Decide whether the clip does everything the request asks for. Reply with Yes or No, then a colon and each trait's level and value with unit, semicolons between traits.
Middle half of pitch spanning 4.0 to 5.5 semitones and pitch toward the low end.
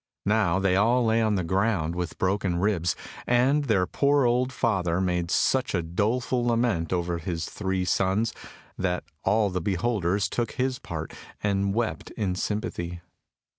Yes: average, 4.5 semitones; low, 100 Hz